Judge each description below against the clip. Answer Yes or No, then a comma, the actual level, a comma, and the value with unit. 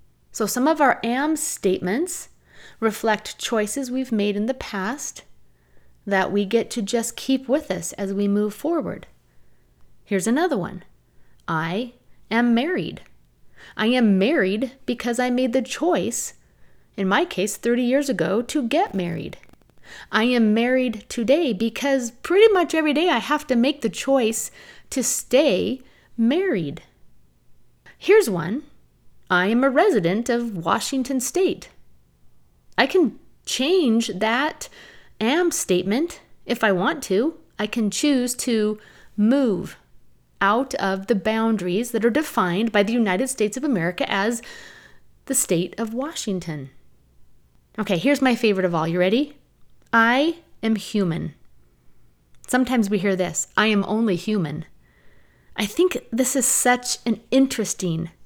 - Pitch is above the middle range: Yes, high, 225 Hz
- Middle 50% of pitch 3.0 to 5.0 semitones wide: No, wide, 5.6 semitones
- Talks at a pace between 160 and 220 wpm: No, average, 140 wpm